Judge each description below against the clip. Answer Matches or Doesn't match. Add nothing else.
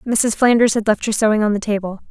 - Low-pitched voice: Doesn't match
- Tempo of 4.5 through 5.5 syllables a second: Doesn't match